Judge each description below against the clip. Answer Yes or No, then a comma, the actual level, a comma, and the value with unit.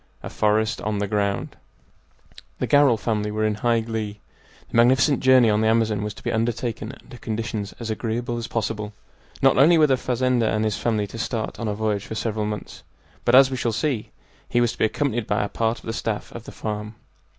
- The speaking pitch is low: Yes, low, 110 Hz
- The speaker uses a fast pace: Yes, fast, 215 wpm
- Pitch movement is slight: Yes, narrow, 2.1 semitones